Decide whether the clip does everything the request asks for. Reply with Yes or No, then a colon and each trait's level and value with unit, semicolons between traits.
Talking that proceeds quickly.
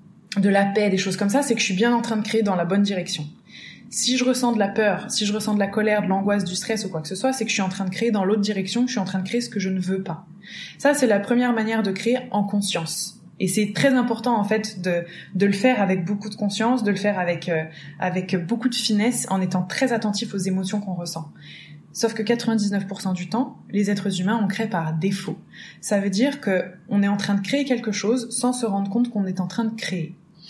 Yes: fast, 270 wpm